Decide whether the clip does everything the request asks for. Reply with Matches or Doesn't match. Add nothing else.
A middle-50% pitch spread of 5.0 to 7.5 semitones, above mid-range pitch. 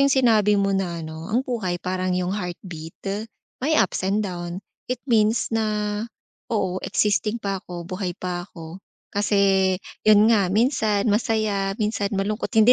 Doesn't match